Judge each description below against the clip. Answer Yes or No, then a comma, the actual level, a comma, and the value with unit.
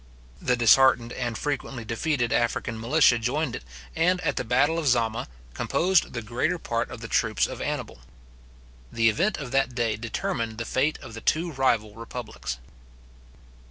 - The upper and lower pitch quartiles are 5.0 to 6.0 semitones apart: No, average, 3.3 semitones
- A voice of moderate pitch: No, low, 120 Hz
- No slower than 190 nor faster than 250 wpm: No, average, 160 wpm